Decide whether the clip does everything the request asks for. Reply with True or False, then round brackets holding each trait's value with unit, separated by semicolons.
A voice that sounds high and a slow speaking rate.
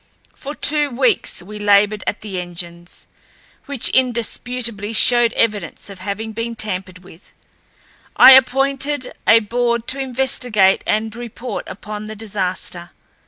True (220 Hz; 125 wpm)